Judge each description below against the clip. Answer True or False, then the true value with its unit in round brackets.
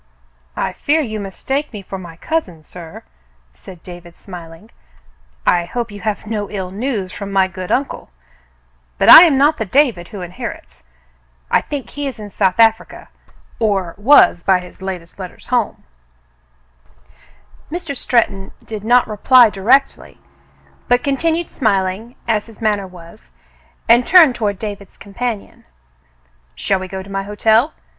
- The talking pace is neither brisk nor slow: True (150 wpm)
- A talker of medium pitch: False (205 Hz)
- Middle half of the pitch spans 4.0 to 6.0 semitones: True (4.7 semitones)